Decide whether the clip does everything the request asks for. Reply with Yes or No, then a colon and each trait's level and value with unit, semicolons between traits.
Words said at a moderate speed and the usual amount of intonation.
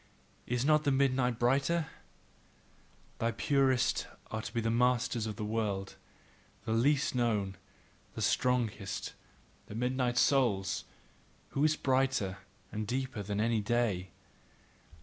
No: slow, 120 wpm; average, 3.6 semitones